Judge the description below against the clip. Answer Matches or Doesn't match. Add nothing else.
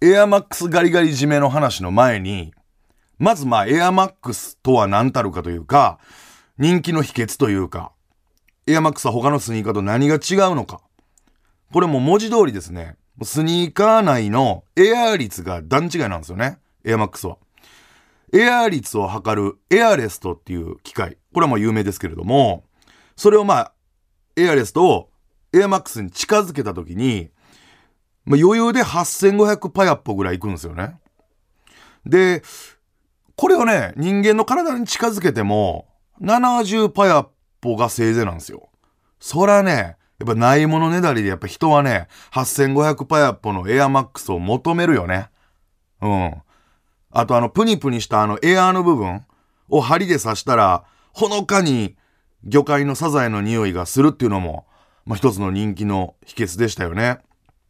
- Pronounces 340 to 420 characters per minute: Doesn't match